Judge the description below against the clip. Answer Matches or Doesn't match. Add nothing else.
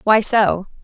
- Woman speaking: Matches